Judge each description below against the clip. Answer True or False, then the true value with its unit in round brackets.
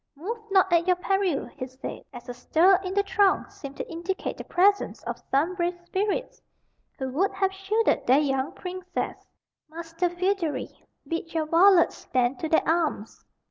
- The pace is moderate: True (170 wpm)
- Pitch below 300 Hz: False (345 Hz)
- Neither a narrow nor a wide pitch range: True (4.2 semitones)